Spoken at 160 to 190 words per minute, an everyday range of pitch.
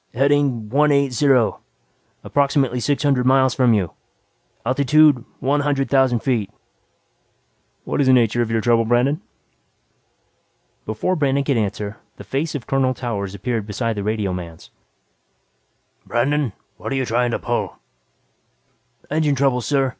No: slow, 135 wpm; average, 3.6 semitones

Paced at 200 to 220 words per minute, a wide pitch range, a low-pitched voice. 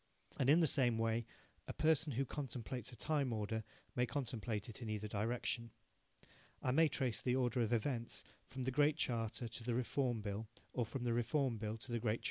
No: fast, 205 wpm; average, 2.8 semitones; low, 120 Hz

